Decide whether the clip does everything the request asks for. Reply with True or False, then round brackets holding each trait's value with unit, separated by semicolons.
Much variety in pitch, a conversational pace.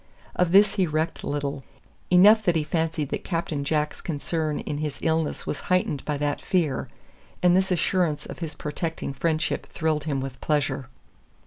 False (2.9 semitones; 165 wpm)